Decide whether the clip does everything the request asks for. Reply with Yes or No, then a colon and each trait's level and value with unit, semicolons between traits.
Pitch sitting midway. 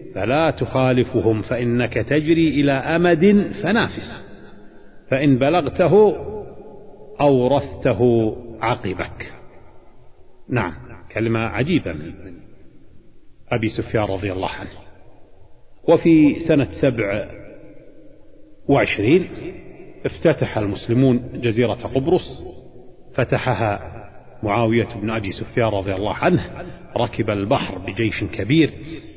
No: low, 120 Hz